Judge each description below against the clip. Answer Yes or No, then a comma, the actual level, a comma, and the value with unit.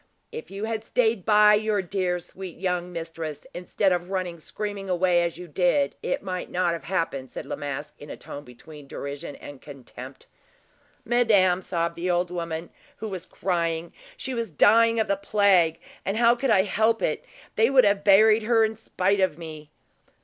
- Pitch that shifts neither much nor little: Yes, average, 4.1 semitones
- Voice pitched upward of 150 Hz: Yes, medium, 185 Hz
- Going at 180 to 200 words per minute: Yes, average, 185 wpm